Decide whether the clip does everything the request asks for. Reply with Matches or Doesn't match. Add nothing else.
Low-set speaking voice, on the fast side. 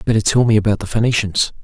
Matches